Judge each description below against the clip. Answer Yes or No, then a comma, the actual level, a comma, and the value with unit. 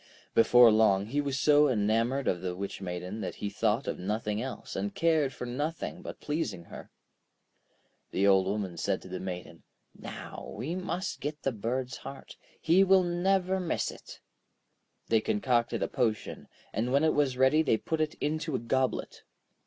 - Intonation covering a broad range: Yes, wide, 6.5 semitones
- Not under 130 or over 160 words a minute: No, average, 175 wpm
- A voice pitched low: Yes, low, 125 Hz